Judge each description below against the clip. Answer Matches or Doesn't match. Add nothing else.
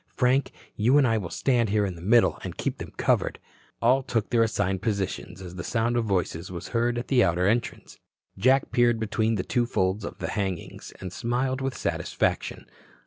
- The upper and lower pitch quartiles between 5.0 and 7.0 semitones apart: Doesn't match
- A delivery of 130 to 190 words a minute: Doesn't match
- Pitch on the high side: Doesn't match